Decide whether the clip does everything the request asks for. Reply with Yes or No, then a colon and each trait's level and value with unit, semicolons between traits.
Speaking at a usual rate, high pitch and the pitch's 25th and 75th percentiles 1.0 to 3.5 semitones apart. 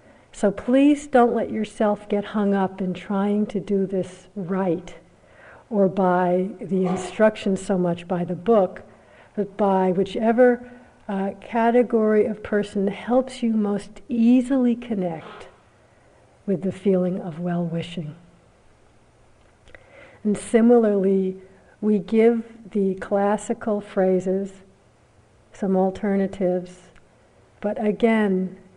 No: slow, 110 wpm; high, 200 Hz; narrow, 2.6 semitones